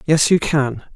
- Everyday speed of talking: Yes, average, 190 wpm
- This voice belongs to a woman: No, male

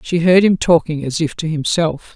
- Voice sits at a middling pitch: Yes, medium, 160 Hz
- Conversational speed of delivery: No, fast, 220 wpm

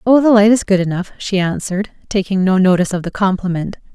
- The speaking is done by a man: No, female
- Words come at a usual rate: No, fast, 215 wpm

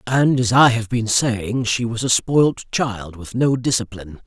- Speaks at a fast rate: No, average, 195 wpm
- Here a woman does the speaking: No, male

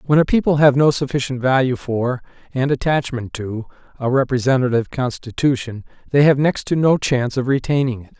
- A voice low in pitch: Yes, low, 130 Hz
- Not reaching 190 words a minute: Yes, average, 170 wpm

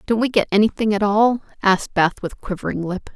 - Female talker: Yes, female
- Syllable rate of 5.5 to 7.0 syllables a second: Yes, 5.8 syllables/s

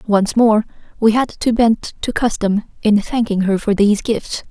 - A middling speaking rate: Yes, average, 185 wpm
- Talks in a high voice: Yes, high, 215 Hz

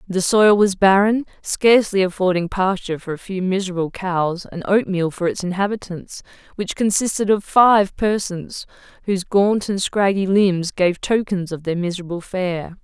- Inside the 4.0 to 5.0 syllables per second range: Yes, 4.8 syllables/s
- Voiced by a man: No, female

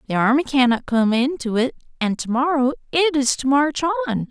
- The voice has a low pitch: No, very high, 270 Hz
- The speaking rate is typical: Yes, average, 195 wpm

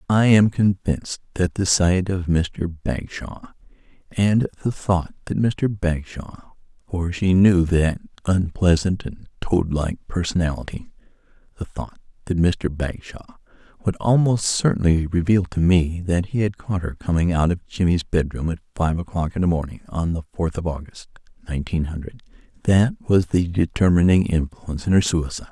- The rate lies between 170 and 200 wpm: No, average, 150 wpm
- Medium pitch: No, very low, 90 Hz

